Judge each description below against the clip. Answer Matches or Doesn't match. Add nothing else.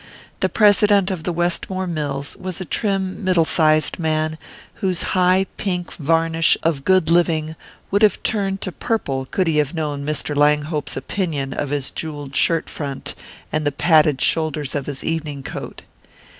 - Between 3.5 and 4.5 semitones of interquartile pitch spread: Matches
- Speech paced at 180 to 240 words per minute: Doesn't match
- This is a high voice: Doesn't match